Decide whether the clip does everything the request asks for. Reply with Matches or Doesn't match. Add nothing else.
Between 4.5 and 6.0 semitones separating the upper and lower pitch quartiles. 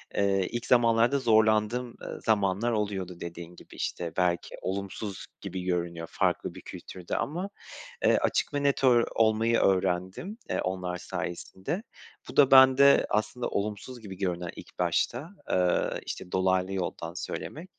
Matches